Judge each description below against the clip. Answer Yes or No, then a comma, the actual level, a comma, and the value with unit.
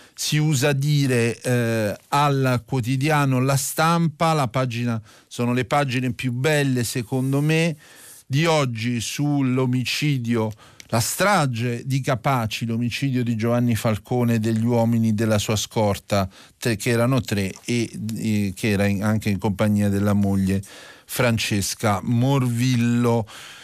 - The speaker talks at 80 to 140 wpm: Yes, average, 125 wpm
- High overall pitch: No, low, 120 Hz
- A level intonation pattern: No, average, 3.4 semitones